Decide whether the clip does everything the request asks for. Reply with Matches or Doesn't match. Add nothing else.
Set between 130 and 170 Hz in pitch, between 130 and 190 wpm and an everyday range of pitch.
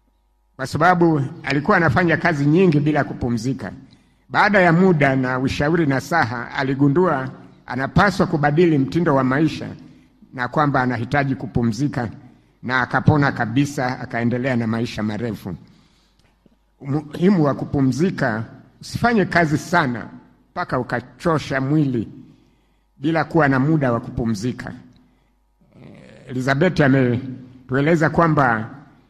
Doesn't match